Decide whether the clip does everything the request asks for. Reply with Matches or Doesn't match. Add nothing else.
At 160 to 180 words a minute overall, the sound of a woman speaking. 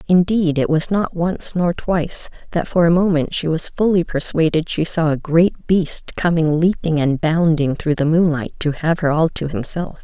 Doesn't match